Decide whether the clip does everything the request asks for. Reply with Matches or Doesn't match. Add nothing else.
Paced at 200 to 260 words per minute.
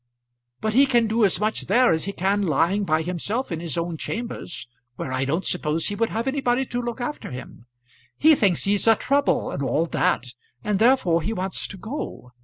Matches